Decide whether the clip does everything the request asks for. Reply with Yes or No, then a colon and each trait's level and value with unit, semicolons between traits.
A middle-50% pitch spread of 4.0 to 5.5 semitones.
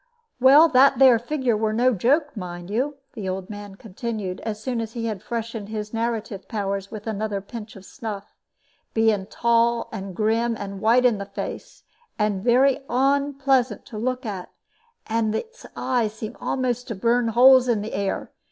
No: average, 3.1 semitones